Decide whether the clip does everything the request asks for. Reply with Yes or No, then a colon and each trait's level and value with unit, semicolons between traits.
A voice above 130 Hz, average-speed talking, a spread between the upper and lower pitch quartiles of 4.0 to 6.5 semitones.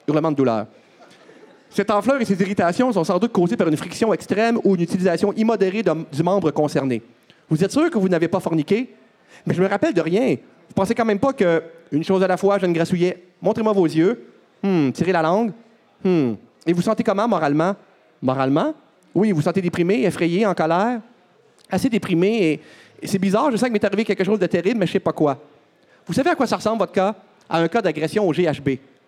No: high, 190 Hz; fast, 225 wpm; average, 4.5 semitones